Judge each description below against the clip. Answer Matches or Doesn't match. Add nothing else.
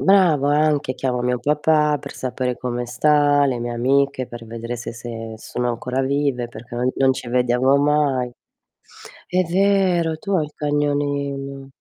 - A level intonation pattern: Doesn't match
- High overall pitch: Doesn't match